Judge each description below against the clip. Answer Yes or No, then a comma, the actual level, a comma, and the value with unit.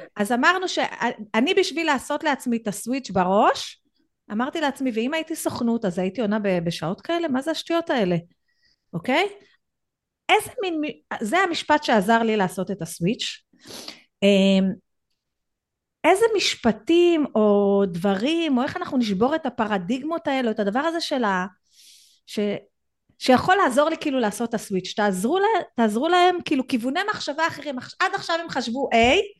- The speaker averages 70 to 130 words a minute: No, average, 140 wpm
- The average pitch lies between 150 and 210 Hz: No, very high, 260 Hz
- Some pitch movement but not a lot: No, wide, 7.6 semitones